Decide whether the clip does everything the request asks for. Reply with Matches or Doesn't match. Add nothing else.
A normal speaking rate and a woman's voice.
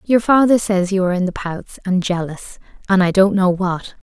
Doesn't match